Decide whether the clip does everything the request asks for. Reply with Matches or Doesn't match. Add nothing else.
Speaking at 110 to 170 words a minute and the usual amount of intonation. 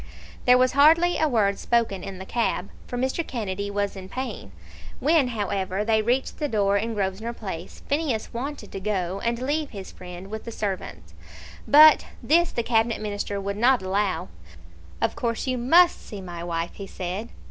Doesn't match